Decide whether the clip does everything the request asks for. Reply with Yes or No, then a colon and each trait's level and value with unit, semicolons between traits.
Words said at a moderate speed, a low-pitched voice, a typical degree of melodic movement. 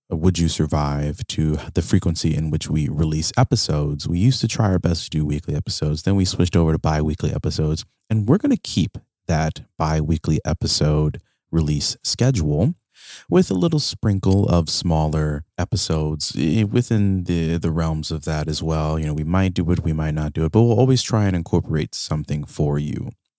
Yes: average, 190 wpm; very low, 80 Hz; average, 4.2 semitones